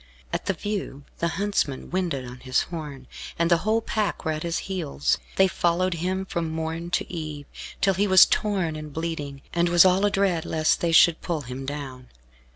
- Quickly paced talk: No, average, 190 wpm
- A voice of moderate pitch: Yes, medium, 170 Hz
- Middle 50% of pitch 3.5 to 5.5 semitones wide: Yes, average, 4.0 semitones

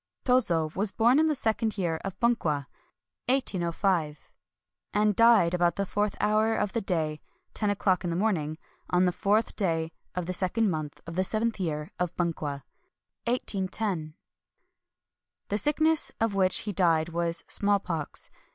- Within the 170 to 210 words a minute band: No, average, 155 wpm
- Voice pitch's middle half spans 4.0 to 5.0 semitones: Yes, average, 4.5 semitones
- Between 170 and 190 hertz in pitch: Yes, medium, 185 Hz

